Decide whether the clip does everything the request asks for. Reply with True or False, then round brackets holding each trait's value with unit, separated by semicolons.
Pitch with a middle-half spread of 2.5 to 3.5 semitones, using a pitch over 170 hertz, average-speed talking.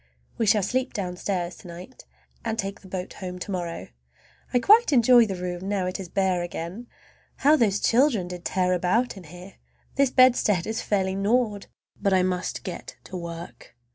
False (4.1 semitones; 190 Hz; 175 wpm)